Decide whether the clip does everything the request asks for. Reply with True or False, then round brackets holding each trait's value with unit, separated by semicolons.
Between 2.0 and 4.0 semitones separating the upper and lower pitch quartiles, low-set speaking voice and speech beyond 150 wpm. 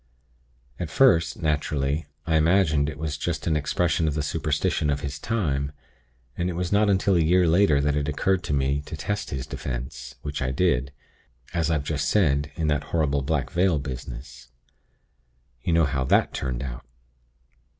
True (3.4 semitones; 75 Hz; 175 wpm)